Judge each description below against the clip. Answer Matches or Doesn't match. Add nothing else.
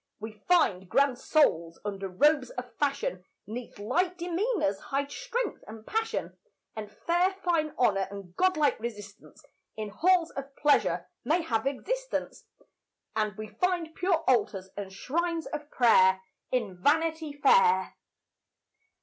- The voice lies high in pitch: Matches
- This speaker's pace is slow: Matches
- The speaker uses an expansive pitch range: Matches